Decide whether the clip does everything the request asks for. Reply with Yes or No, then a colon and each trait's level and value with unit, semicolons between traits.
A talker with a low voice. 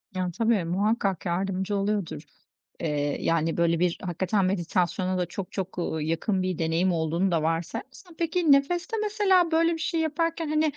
No: high, 190 Hz